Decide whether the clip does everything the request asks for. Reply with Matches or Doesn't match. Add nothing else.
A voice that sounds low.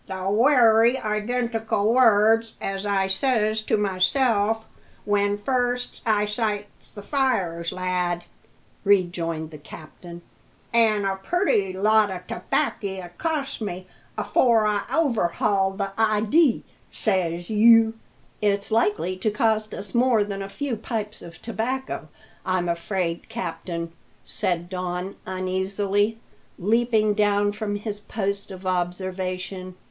Doesn't match